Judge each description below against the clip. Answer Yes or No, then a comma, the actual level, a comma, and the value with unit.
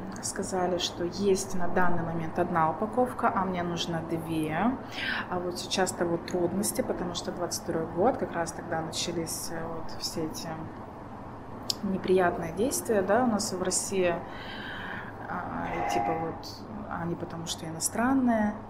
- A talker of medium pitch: Yes, medium, 175 Hz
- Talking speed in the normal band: Yes, average, 140 wpm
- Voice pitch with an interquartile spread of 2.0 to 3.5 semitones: Yes, average, 3.1 semitones